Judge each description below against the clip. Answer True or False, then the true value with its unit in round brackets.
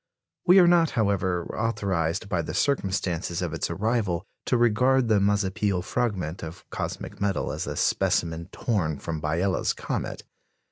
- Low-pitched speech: True (95 Hz)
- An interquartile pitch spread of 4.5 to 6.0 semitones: True (5.0 semitones)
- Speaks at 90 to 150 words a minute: True (145 wpm)